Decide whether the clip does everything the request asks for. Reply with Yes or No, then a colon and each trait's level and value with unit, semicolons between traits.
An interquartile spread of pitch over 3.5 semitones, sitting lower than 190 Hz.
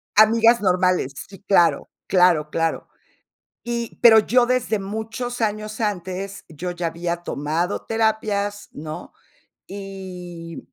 No: average, 3.9 semitones; high, 195 Hz